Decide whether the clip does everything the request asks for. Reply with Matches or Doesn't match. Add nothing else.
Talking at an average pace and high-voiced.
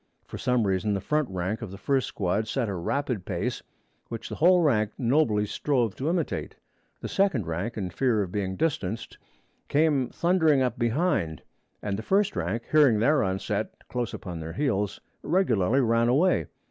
Doesn't match